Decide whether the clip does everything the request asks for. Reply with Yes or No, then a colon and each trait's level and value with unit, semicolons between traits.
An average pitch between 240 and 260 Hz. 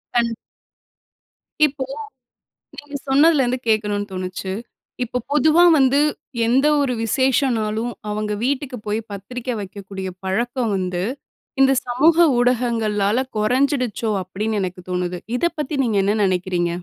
No: high, 230 Hz